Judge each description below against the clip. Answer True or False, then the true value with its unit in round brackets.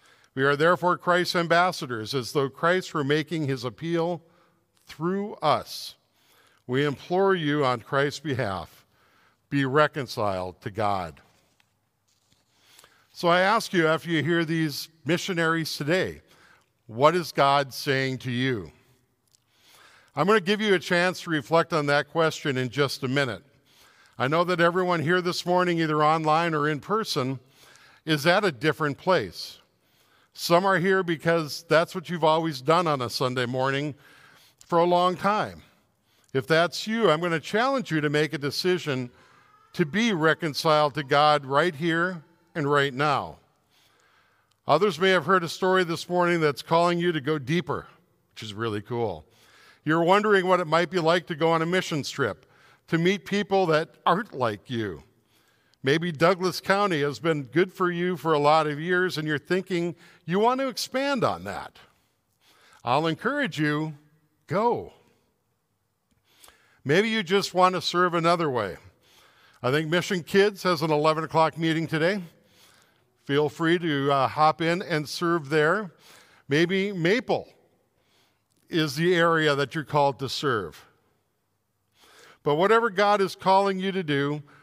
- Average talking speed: True (155 wpm)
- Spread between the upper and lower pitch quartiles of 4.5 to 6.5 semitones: False (3.8 semitones)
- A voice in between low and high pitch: True (160 Hz)